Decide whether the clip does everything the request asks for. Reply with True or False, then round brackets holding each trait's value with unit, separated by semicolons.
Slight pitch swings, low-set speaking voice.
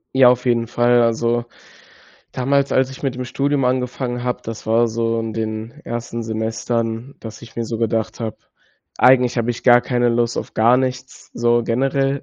True (1.7 semitones; 120 Hz)